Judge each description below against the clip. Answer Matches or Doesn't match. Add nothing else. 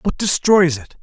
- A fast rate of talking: Doesn't match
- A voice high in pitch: Doesn't match